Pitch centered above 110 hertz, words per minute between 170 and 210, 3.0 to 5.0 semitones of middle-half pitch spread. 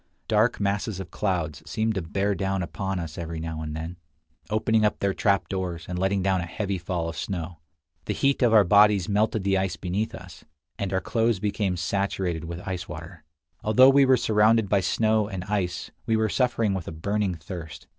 No: very low, 95 Hz; average, 195 wpm; average, 3.4 semitones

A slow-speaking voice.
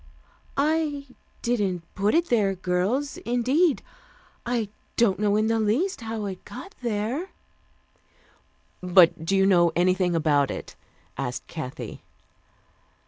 Yes: slow, 125 wpm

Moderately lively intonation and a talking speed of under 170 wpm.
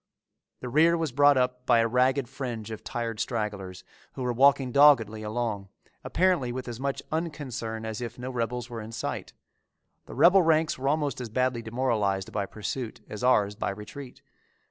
No: average, 3.6 semitones; average, 175 wpm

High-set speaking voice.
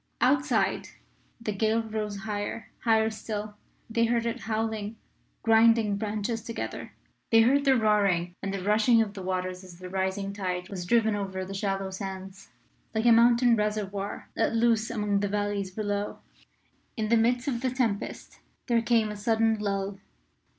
Yes: high, 215 Hz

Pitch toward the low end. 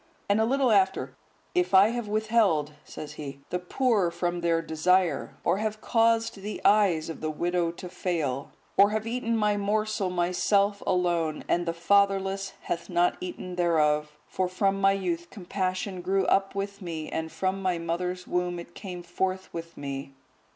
No: medium, 185 Hz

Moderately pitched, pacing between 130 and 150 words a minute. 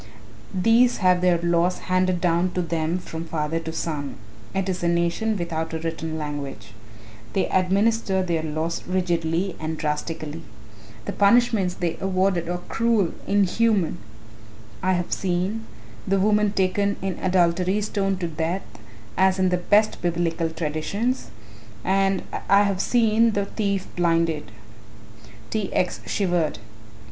Yes: medium, 180 Hz; slow, 135 wpm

